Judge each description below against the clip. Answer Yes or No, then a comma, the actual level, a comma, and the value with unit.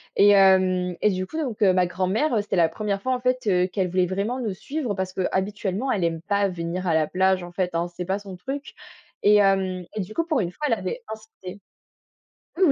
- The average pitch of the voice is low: No, high, 190 Hz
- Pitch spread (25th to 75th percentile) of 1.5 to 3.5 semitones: Yes, average, 2.8 semitones